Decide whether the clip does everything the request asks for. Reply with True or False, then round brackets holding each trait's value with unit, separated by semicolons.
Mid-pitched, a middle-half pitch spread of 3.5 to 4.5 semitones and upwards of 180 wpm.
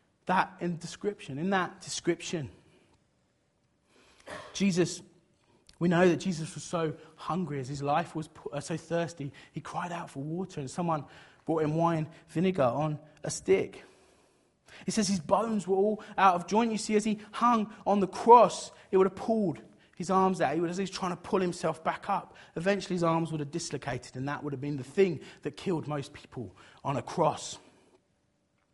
True (170 Hz; 4.1 semitones; 190 wpm)